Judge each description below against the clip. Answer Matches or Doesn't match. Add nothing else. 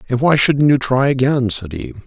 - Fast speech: Matches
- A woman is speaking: Doesn't match